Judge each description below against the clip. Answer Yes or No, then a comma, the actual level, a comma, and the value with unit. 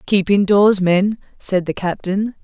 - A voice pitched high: Yes, high, 195 Hz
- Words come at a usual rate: Yes, average, 150 wpm